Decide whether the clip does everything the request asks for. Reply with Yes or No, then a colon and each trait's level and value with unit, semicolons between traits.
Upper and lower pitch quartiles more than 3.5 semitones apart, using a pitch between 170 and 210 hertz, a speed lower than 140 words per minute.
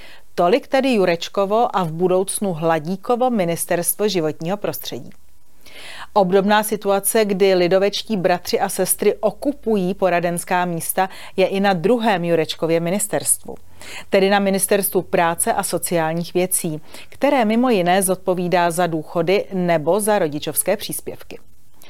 No: average, 2.8 semitones; high, 190 Hz; average, 120 wpm